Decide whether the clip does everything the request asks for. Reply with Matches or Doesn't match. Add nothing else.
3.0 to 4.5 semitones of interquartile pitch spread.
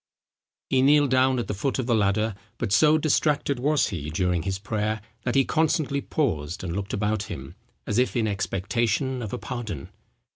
Doesn't match